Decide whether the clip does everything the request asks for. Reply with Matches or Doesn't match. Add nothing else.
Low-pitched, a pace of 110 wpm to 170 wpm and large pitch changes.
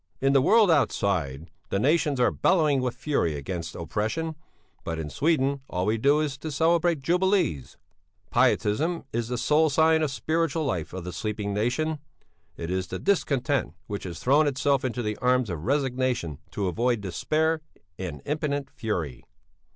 Matches